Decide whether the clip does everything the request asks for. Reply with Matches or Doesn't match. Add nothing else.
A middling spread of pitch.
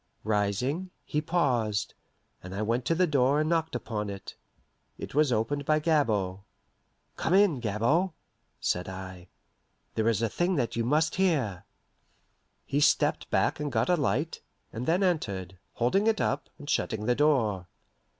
Doesn't match